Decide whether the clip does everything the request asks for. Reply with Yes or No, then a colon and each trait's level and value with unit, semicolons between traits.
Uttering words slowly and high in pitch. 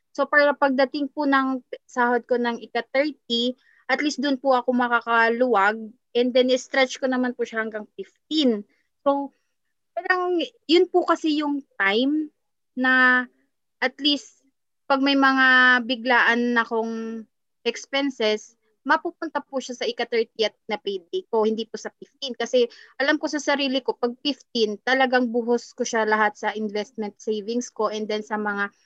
No: fast, 155 wpm; very high, 250 Hz